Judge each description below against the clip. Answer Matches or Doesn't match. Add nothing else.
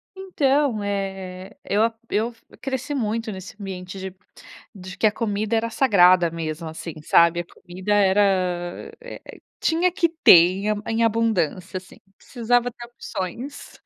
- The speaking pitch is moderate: Doesn't match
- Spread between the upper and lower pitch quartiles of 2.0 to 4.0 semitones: Doesn't match